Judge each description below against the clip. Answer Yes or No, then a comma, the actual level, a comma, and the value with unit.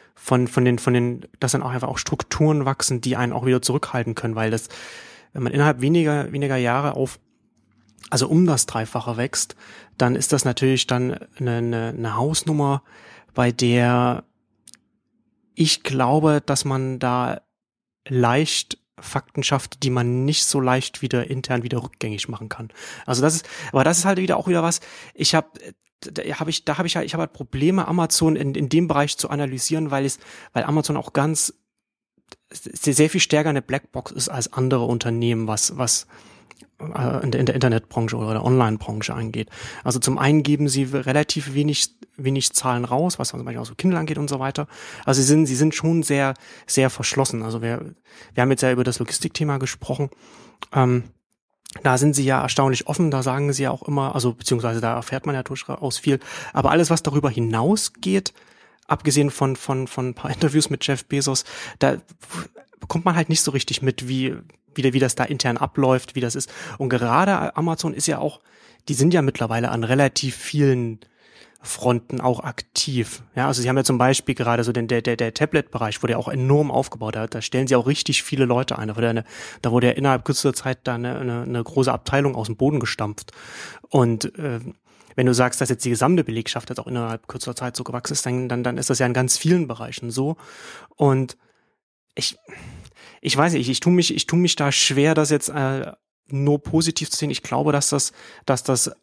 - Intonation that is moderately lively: Yes, average, 3.2 semitones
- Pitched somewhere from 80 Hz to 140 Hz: Yes, low, 135 Hz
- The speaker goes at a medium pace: No, fast, 200 wpm